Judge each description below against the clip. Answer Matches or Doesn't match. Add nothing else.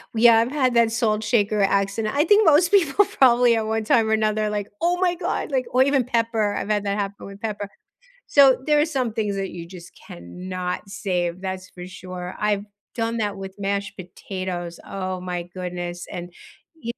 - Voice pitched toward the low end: Doesn't match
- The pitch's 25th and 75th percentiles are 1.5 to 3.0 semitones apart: Doesn't match